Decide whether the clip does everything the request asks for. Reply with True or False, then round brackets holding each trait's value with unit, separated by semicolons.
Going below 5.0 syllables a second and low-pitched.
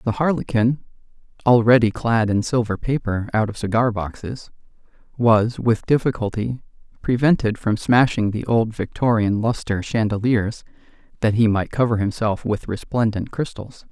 True (4.7 syllables/s; 115 Hz)